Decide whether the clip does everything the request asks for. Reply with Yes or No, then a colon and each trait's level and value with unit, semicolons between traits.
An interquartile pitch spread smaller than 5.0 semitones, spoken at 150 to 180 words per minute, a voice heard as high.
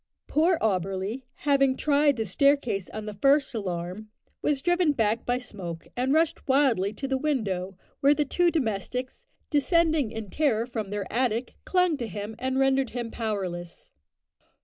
No: wide, 5.5 semitones; average, 155 wpm; very high, 250 Hz